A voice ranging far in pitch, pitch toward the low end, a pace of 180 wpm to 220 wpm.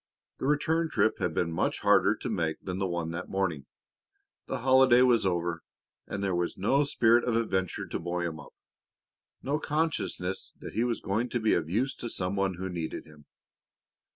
Yes: wide, 6.0 semitones; very low, 95 Hz; average, 190 wpm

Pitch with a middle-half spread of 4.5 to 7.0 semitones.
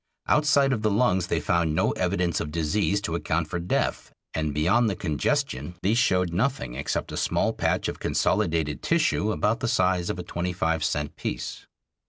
Yes: average, 5.1 semitones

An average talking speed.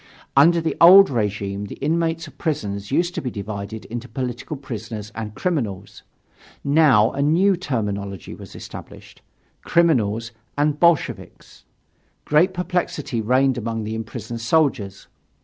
No: slow, 130 wpm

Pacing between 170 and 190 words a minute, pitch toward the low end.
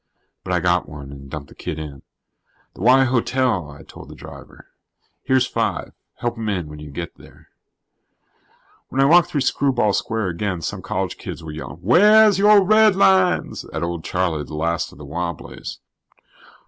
Yes: average, 175 wpm; very low, 95 Hz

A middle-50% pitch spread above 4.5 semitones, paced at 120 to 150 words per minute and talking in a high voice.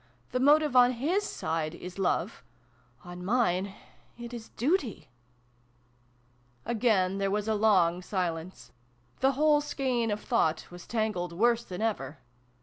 Yes: wide, 5.5 semitones; average, 140 wpm; high, 205 Hz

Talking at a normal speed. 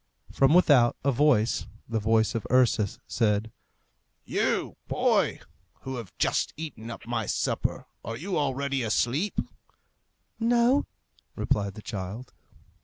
No: slow, 120 wpm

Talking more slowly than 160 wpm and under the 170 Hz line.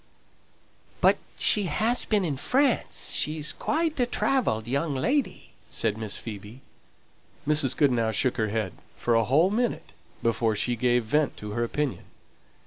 Yes: average, 145 wpm; low, 135 Hz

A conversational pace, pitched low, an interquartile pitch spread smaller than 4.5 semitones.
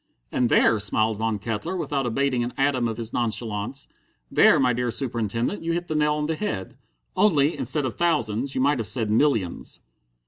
No: average, 185 wpm; low, 125 Hz; average, 4.8 semitones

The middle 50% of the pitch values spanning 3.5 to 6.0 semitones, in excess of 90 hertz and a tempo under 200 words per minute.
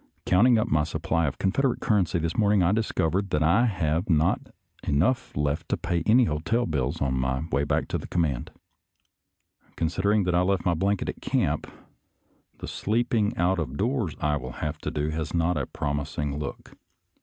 No: average, 5.1 semitones; very low, 85 Hz; average, 190 wpm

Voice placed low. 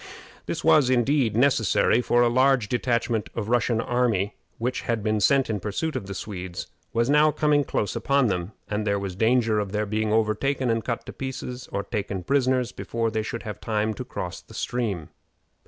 Yes: low, 115 Hz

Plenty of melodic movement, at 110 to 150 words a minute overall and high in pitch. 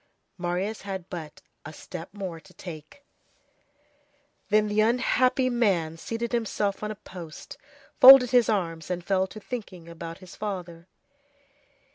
No: average, 4.6 semitones; average, 140 wpm; high, 195 Hz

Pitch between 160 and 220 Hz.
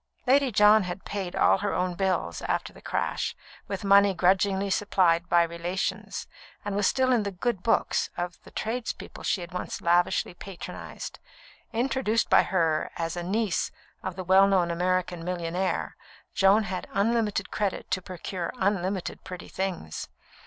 Yes: high, 190 Hz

